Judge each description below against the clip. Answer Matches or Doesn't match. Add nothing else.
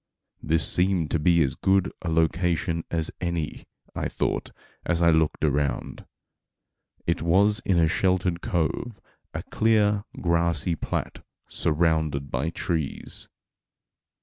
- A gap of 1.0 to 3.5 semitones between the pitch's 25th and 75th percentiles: Matches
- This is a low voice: Matches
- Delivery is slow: Matches